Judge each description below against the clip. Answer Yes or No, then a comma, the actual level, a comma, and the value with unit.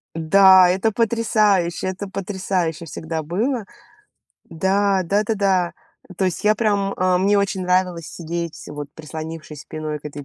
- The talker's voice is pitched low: No, medium, 185 Hz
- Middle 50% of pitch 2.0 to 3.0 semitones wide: No, average, 3.4 semitones